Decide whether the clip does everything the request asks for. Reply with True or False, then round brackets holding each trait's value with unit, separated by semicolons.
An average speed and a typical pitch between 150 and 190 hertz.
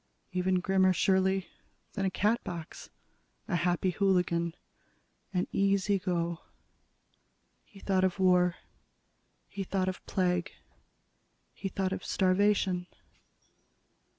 False (100 wpm; 185 Hz)